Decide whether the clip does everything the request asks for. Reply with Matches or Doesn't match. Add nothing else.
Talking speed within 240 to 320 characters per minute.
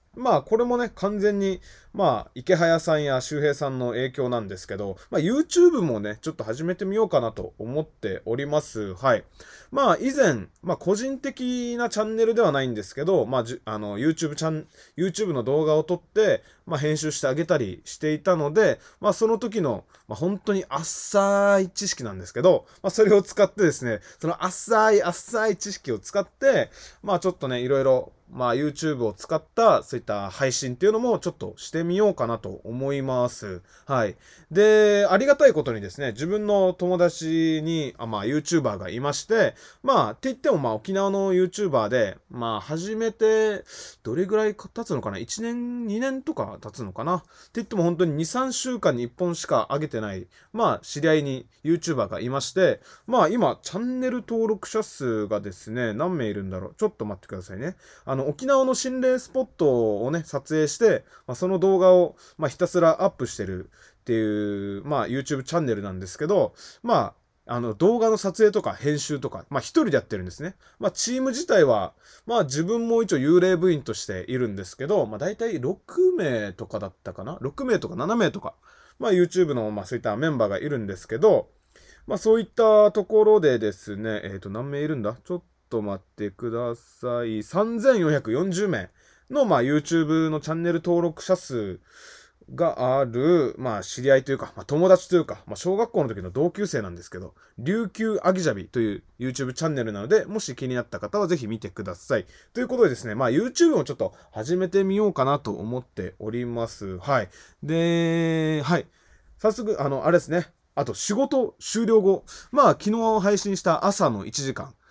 Doesn't match